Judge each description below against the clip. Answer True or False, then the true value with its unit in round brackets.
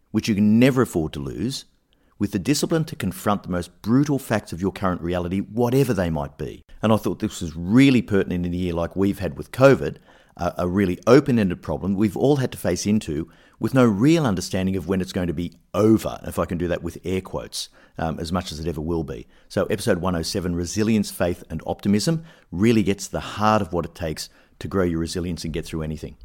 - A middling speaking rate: False (230 wpm)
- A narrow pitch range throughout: False (4.1 semitones)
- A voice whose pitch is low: True (95 Hz)